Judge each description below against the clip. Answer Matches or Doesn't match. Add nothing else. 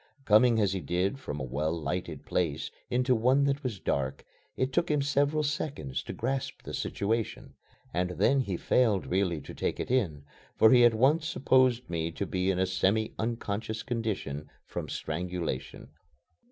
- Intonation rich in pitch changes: Matches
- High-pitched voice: Doesn't match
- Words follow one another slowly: Doesn't match